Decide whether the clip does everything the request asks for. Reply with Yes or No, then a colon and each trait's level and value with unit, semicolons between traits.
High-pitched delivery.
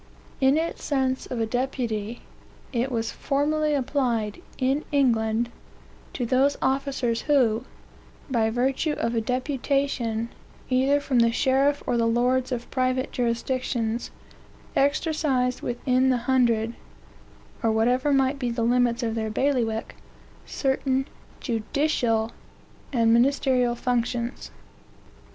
Yes: very high, 250 Hz